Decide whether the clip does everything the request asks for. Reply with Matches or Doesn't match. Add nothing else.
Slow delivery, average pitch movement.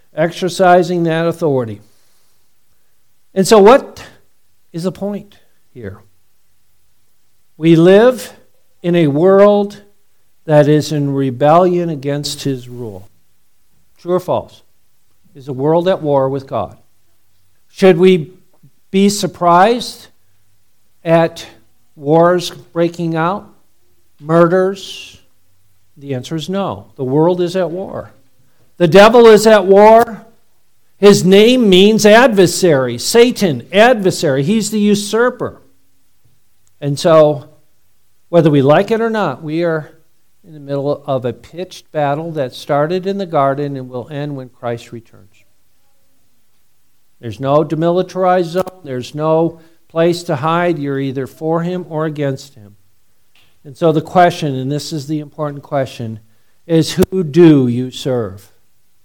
Doesn't match